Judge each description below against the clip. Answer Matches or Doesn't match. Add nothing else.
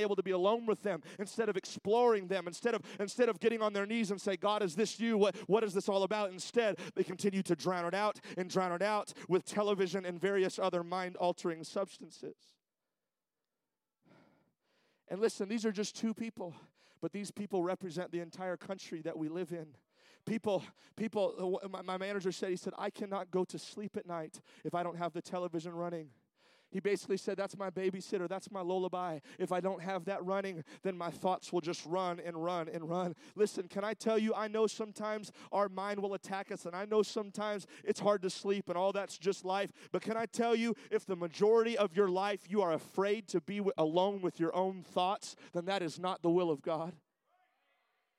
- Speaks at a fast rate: Matches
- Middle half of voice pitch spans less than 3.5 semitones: Matches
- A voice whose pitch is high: Matches